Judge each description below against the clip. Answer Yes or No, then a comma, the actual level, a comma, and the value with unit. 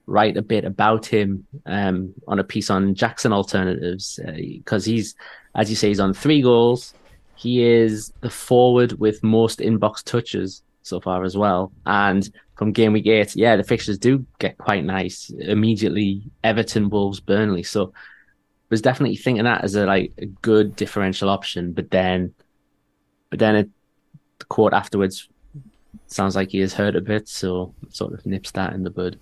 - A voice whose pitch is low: Yes, low, 105 Hz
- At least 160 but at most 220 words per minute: Yes, average, 175 wpm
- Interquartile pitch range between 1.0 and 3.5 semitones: Yes, narrow, 2.6 semitones